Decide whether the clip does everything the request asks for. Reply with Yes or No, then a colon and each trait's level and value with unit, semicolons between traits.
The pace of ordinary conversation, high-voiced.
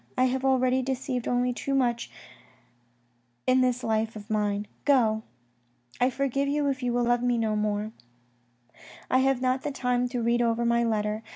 Yes: average, 170 wpm; high, 245 Hz